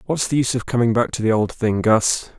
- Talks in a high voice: No, low, 115 Hz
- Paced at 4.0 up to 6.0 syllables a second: Yes, 5.9 syllables/s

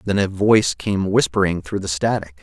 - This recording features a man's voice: Yes, male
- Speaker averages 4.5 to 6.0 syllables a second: Yes, 5.3 syllables/s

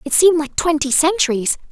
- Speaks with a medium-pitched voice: No, very high, 305 Hz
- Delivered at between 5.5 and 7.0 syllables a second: Yes, 6.0 syllables/s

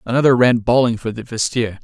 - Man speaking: Yes, male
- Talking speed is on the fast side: No, average, 195 wpm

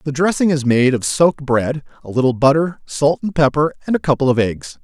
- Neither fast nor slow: No, fast, 225 wpm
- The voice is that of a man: Yes, male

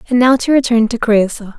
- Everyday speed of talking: No, fast, 225 wpm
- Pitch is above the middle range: Yes, high, 235 Hz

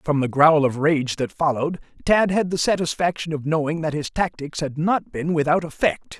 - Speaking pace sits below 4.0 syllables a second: No, 5.1 syllables/s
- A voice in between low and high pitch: Yes, medium, 155 Hz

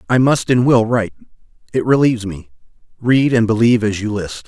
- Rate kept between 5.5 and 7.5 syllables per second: Yes, 5.9 syllables/s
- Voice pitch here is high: No, low, 115 Hz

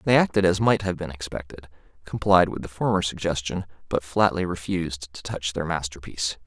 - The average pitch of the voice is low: Yes, very low, 85 Hz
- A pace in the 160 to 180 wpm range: Yes, average, 175 wpm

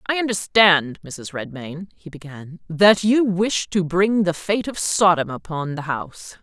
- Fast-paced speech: No, average, 170 wpm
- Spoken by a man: No, female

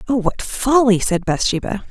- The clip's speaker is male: No, female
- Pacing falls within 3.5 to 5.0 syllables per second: Yes, 4.7 syllables/s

